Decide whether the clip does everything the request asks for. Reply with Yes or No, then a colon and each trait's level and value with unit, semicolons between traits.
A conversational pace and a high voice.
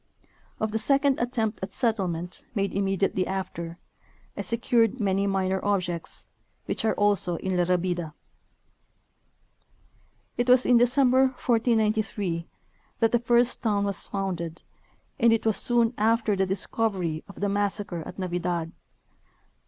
No: slow, 130 wpm; high, 200 Hz